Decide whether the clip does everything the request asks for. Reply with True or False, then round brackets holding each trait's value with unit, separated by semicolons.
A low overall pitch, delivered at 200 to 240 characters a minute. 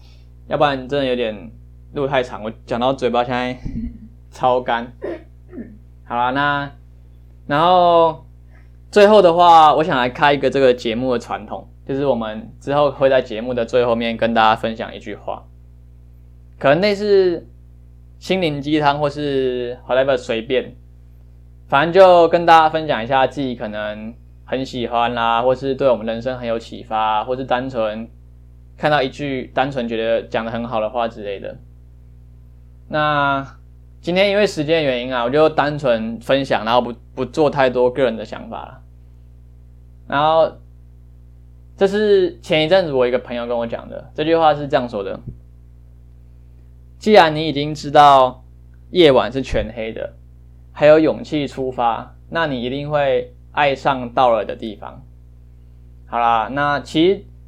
True (120 Hz; 235 characters per minute)